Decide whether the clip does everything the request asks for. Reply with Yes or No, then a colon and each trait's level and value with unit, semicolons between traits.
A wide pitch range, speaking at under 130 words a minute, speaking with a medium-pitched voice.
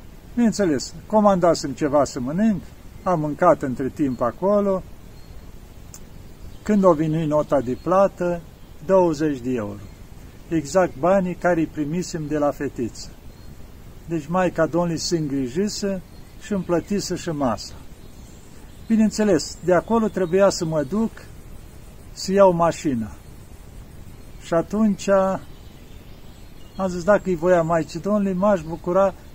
Yes: wide, 6.7 semitones; average, 120 wpm; medium, 170 Hz